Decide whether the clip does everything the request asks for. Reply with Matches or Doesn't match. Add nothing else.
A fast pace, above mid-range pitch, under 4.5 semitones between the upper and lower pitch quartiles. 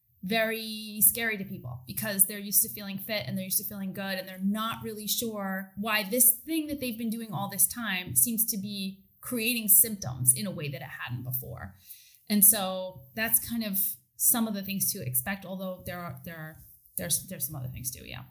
Doesn't match